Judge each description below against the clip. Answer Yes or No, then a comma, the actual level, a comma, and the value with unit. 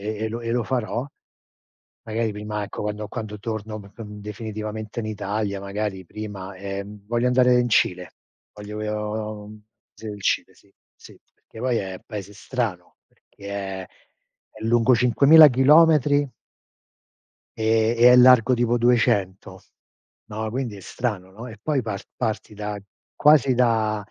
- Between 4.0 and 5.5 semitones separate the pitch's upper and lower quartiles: No, average, 2.7 semitones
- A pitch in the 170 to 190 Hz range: No, low, 110 Hz